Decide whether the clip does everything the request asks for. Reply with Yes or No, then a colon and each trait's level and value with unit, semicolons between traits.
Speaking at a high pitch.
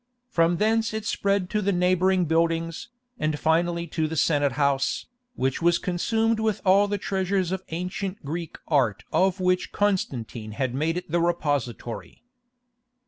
No: medium, 175 Hz